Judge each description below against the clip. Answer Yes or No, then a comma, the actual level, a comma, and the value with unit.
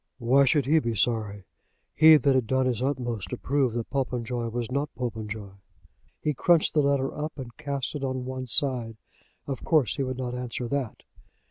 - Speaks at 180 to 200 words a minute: Yes, average, 190 wpm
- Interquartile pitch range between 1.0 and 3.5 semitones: Yes, average, 3.0 semitones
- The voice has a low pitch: Yes, low, 130 Hz